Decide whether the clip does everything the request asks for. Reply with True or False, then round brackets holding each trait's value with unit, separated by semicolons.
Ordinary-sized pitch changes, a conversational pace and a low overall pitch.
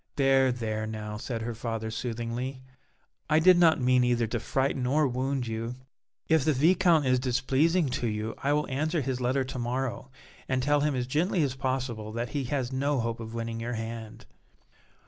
True (3.2 semitones; 185 wpm; 130 Hz)